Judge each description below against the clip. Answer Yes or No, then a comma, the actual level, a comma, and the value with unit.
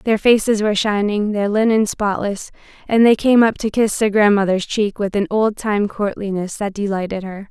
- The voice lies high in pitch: Yes, high, 205 Hz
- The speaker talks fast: No, average, 190 wpm